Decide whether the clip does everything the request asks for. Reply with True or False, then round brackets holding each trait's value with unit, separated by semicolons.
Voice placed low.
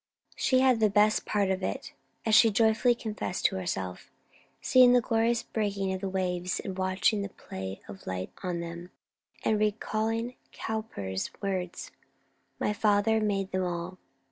False (200 Hz)